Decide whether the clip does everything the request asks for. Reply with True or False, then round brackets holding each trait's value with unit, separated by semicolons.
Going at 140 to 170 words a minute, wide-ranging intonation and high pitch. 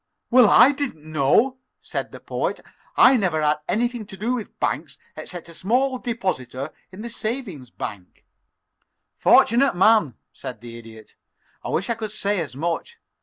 True (165 wpm; 8.1 semitones; 200 Hz)